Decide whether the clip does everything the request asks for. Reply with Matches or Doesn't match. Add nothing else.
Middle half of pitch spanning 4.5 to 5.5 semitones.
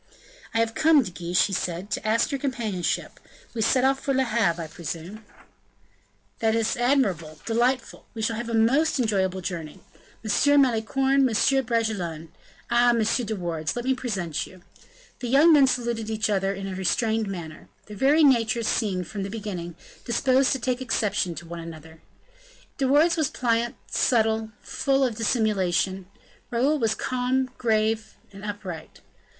Matches